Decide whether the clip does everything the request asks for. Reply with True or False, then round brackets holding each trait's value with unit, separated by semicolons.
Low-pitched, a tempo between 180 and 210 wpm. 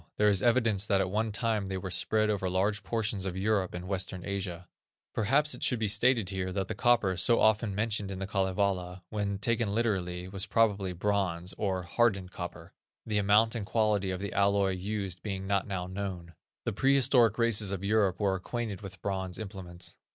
True (100 Hz; 190 wpm)